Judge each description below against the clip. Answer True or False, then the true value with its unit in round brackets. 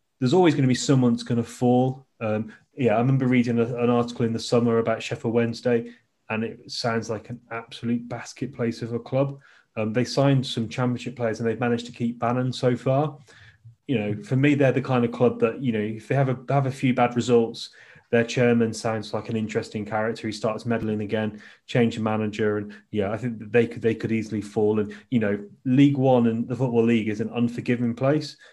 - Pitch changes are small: True (2.0 semitones)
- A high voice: False (120 Hz)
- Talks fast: True (225 wpm)